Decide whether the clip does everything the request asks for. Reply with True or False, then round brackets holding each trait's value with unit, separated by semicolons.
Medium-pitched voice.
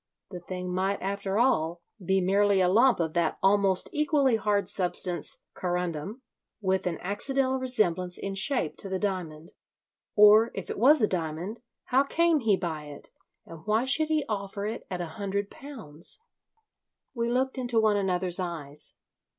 False (195 Hz)